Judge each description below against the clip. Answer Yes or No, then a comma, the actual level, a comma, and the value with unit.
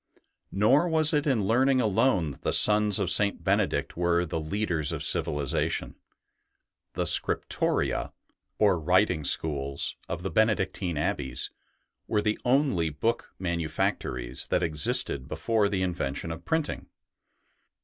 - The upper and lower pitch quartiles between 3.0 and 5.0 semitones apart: No, wide, 5.4 semitones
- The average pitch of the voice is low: Yes, very low, 95 Hz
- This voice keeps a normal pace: No, slow, 130 wpm